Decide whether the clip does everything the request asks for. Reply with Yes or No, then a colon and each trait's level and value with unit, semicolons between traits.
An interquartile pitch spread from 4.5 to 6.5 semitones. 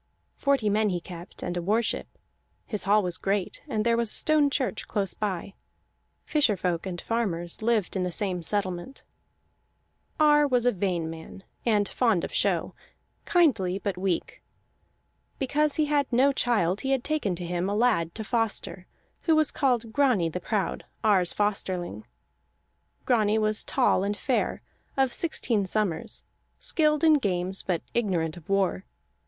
Yes: wide, 5.4 semitones